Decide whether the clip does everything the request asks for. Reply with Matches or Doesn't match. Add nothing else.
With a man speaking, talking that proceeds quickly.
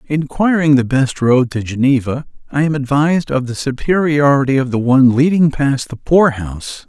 Doesn't match